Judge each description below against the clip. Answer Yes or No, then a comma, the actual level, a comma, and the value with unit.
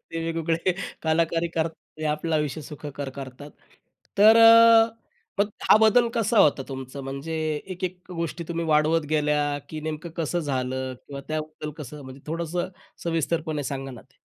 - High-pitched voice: No, medium, 155 Hz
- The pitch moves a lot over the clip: No, average, 2.8 semitones